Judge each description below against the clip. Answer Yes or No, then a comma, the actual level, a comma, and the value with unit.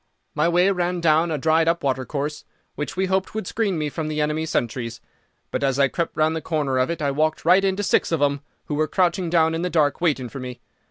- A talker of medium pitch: Yes, medium, 155 Hz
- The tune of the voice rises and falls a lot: No, average, 3.2 semitones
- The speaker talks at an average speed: No, fast, 240 wpm